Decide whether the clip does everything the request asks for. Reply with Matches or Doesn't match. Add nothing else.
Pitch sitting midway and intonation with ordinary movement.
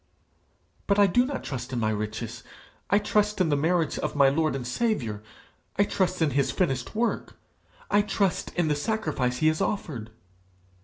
Doesn't match